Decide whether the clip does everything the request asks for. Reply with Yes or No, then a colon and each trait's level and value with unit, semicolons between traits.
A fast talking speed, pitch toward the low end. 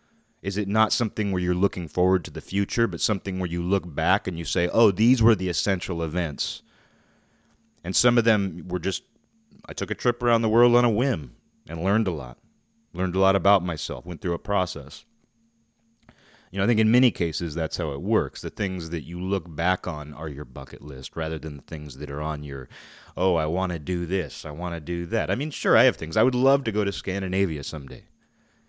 Yes: fast, 230 wpm; very low, 90 Hz